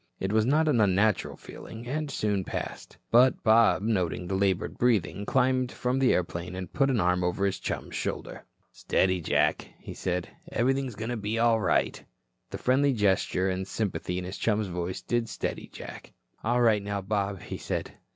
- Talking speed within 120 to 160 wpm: No, average, 185 wpm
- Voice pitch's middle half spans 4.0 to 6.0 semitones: Yes, average, 4.4 semitones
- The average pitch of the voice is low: Yes, low, 105 Hz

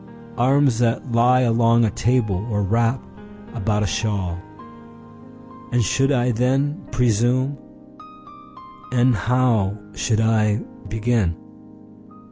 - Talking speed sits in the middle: No, slow, 95 wpm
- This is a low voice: Yes, low, 115 Hz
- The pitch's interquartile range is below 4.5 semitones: Yes, average, 2.9 semitones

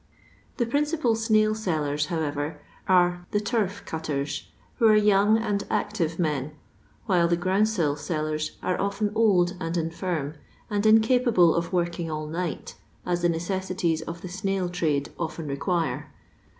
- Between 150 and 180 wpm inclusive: No, average, 140 wpm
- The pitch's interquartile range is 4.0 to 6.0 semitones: Yes, average, 4.4 semitones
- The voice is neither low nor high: Yes, medium, 175 Hz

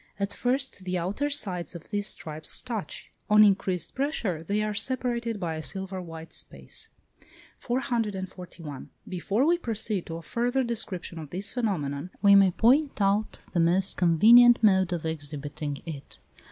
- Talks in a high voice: Yes, high, 195 Hz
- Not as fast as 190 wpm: Yes, average, 155 wpm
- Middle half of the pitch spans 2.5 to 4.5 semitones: No, wide, 5.5 semitones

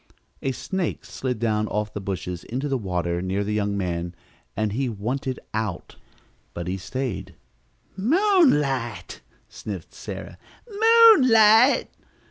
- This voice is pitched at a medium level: No, low, 115 Hz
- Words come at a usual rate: No, slow, 120 wpm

